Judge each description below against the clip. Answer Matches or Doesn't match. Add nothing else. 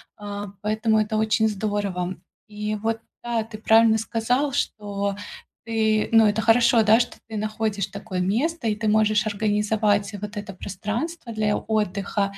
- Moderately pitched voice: Doesn't match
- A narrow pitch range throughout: Matches